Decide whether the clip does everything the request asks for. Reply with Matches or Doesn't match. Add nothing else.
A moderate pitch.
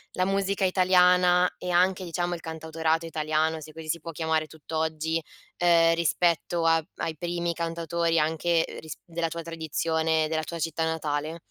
Matches